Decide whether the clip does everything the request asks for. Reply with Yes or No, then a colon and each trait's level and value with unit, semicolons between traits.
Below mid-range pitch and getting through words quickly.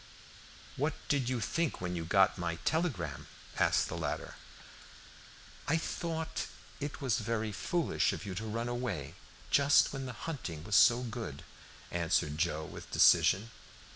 No: low, 115 Hz; average, 145 wpm